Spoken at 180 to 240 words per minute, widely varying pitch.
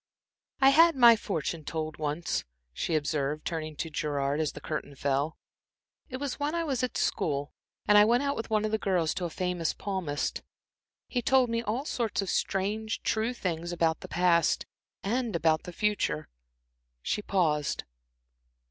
No: average, 165 wpm; wide, 6.7 semitones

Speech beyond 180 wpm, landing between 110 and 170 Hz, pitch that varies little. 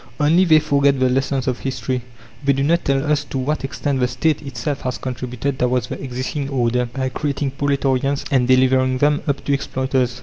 Yes: average, 195 wpm; low, 135 Hz; narrow, 1.8 semitones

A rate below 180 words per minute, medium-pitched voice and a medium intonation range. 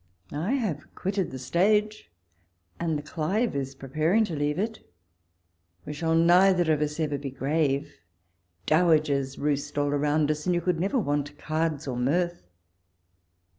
Yes: average, 155 wpm; medium, 155 Hz; average, 3.6 semitones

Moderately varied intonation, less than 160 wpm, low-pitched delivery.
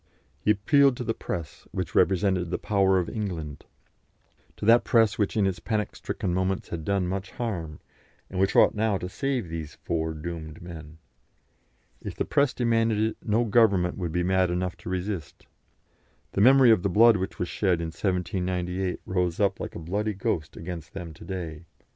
No: average, 3.6 semitones; average, 185 wpm; very low, 95 Hz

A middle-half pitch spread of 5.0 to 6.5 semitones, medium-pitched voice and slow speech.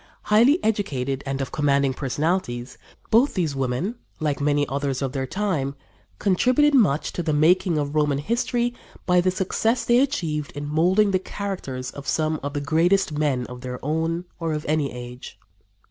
No: wide, 5.4 semitones; medium, 155 Hz; average, 170 wpm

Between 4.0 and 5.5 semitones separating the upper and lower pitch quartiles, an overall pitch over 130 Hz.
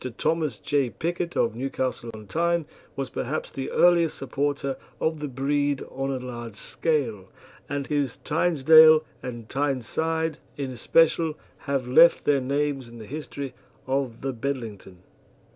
No: average, 3.6 semitones; medium, 140 Hz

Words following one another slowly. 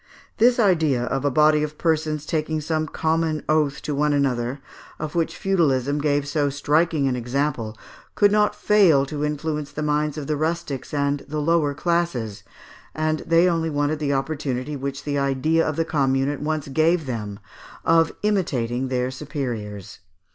No: average, 165 wpm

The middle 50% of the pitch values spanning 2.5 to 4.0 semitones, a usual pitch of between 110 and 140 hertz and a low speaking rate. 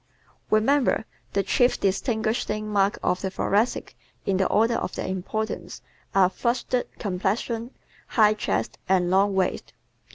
No: average, 2.9 semitones; high, 210 Hz; slow, 130 wpm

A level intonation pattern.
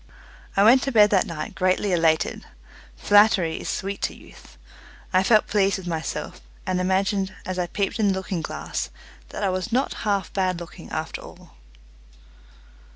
Yes: narrow, 2.1 semitones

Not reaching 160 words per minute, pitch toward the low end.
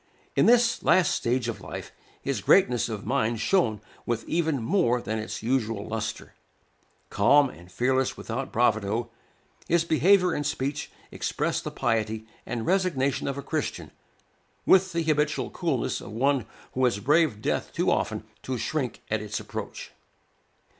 Yes: average, 150 wpm; low, 125 Hz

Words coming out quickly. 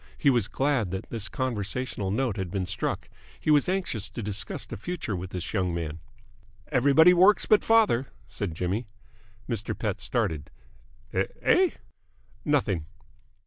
No: average, 145 wpm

